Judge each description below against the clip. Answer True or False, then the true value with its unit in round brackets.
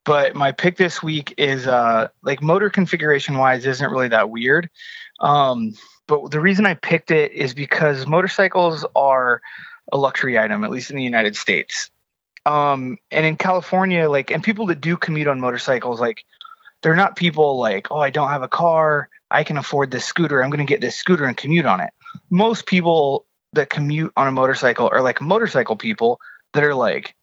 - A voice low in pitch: False (155 Hz)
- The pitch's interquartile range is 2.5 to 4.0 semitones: False (5.1 semitones)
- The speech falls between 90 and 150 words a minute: False (190 wpm)